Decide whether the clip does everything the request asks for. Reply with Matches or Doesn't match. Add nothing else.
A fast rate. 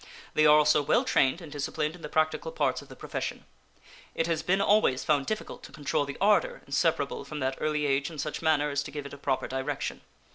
Matches